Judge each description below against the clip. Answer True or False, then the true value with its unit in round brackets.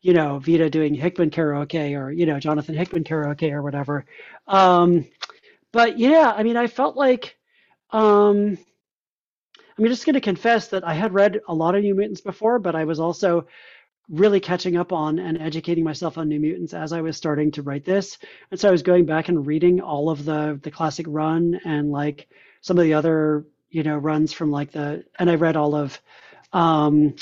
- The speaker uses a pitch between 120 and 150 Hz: False (165 Hz)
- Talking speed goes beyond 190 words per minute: True (200 wpm)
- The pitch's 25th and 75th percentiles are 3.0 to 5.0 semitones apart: True (4.0 semitones)